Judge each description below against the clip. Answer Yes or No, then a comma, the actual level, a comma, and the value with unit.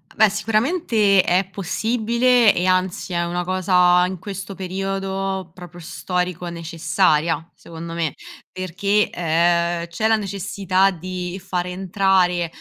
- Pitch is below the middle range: No, medium, 185 Hz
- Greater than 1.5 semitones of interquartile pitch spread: Yes, narrow, 2.2 semitones